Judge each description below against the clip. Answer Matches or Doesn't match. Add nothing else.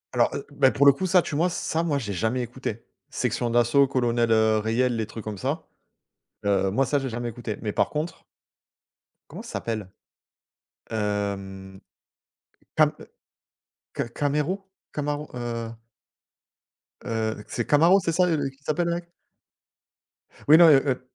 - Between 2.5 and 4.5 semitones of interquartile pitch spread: Doesn't match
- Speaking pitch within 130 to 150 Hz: Doesn't match